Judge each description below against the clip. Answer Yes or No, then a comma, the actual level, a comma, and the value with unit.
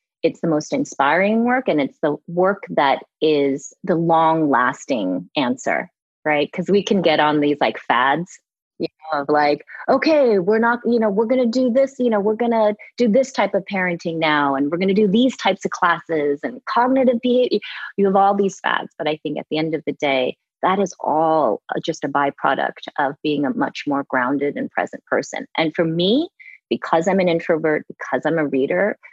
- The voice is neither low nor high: Yes, medium, 175 Hz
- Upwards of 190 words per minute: Yes, average, 200 wpm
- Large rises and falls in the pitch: Yes, wide, 6.7 semitones